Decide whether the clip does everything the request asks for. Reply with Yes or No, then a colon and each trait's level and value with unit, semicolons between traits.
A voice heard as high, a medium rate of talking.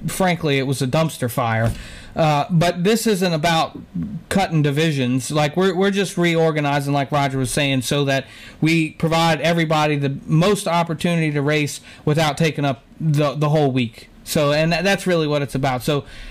No: medium, 150 Hz; average, 175 wpm